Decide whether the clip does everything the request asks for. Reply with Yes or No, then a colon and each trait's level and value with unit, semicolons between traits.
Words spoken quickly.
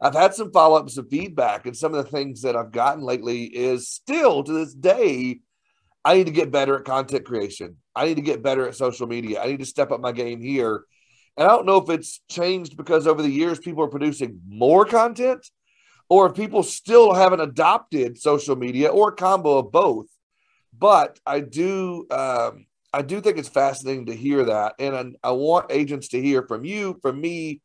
Yes: fast, 210 wpm